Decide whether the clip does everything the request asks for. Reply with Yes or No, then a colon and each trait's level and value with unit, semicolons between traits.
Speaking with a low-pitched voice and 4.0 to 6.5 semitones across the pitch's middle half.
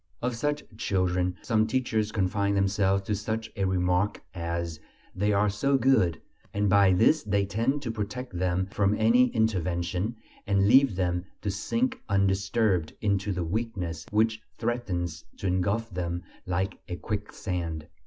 No: low, 100 Hz; average, 3.5 semitones